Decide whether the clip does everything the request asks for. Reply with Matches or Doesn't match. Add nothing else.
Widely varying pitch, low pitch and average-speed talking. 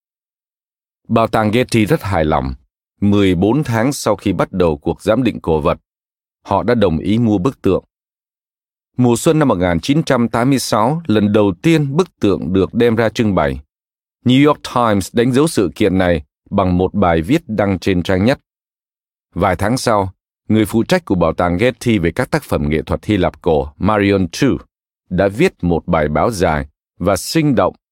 Matches